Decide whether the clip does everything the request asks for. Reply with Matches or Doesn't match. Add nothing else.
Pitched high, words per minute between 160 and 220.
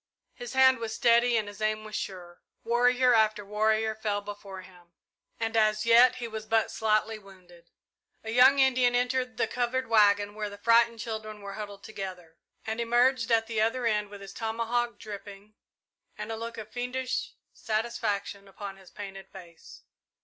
Matches